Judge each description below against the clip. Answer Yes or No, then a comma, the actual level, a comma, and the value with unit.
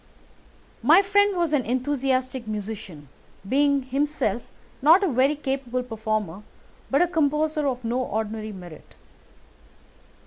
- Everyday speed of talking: No, slow, 125 wpm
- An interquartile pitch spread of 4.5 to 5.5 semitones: Yes, average, 5.1 semitones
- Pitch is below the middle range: No, very high, 260 Hz